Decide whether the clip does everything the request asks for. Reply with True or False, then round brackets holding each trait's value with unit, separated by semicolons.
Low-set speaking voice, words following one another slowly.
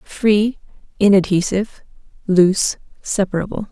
False (195 Hz; 65 wpm)